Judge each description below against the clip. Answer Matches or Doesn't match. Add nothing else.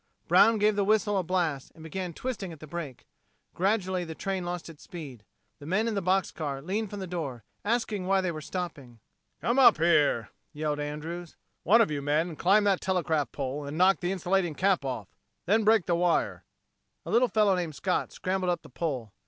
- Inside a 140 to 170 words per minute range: Doesn't match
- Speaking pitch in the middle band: Matches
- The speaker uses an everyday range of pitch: Matches